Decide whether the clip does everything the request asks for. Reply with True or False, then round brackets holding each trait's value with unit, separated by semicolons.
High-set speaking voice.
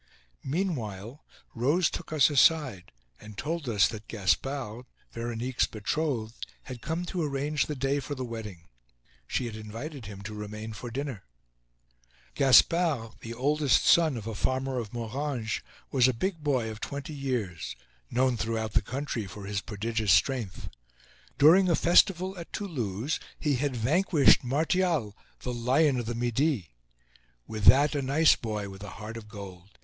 False (125 Hz)